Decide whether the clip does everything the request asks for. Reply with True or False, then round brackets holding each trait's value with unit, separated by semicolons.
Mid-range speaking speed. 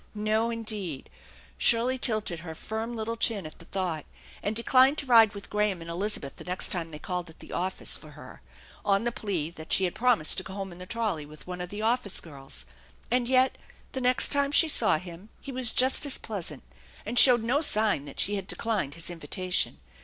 False (215 wpm)